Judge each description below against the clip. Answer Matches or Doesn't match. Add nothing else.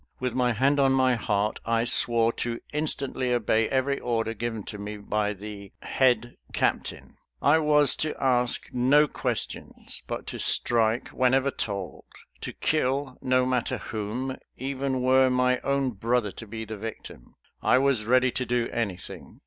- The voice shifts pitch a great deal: Doesn't match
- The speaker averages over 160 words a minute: Doesn't match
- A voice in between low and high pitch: Doesn't match